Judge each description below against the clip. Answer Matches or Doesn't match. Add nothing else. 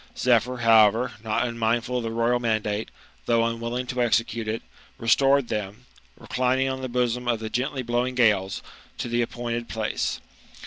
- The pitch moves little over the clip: Matches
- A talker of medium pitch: Doesn't match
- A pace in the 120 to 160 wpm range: Matches